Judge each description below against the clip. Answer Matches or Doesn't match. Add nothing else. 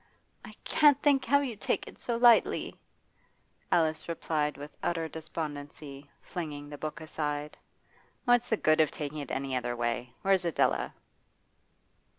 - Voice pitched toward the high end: Doesn't match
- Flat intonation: Doesn't match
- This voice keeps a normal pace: Matches